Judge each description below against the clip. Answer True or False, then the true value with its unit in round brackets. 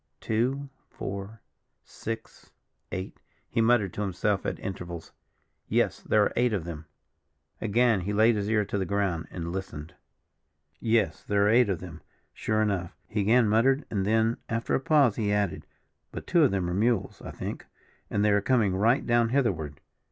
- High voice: False (105 Hz)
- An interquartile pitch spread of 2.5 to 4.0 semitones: True (3.3 semitones)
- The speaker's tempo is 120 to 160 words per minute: False (175 wpm)